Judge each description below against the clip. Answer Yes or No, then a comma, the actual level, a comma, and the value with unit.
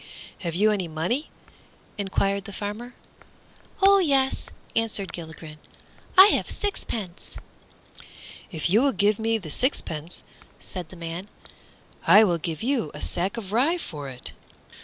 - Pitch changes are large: Yes, wide, 5.8 semitones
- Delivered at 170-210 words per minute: No, average, 140 wpm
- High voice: Yes, high, 200 Hz